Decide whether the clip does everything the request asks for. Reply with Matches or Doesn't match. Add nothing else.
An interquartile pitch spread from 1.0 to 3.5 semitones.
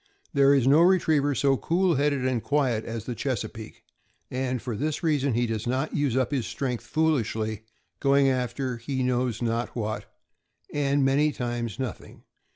Matches